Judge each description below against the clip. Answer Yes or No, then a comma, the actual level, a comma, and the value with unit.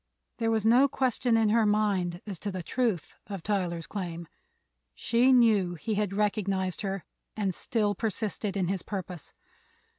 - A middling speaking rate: Yes, average, 155 wpm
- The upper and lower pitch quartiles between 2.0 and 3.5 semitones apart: Yes, average, 3.2 semitones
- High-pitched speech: Yes, high, 205 Hz